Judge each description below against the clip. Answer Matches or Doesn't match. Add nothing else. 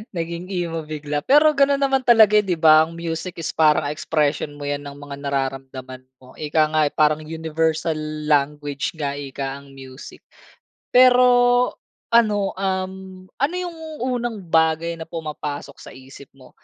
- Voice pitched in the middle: Matches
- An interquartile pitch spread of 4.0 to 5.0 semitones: Matches